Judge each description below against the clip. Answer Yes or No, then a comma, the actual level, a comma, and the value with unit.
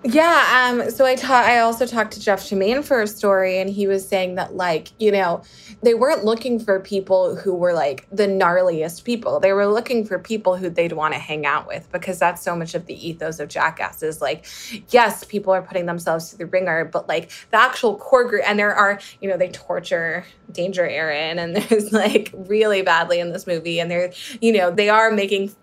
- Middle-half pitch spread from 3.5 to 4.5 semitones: Yes, average, 3.9 semitones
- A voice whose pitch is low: No, high, 195 Hz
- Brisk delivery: Yes, fast, 220 wpm